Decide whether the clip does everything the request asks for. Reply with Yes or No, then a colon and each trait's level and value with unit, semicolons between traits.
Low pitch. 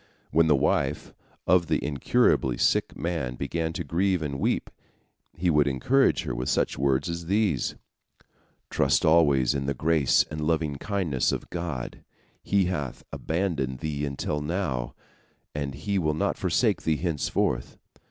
Yes: very low, 75 Hz